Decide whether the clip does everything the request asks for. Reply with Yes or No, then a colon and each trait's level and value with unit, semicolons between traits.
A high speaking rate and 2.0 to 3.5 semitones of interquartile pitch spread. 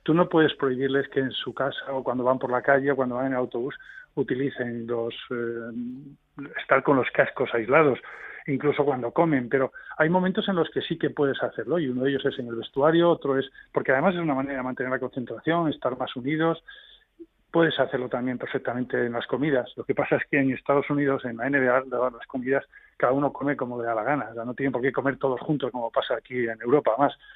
Yes: fast, 230 wpm; average, 2.9 semitones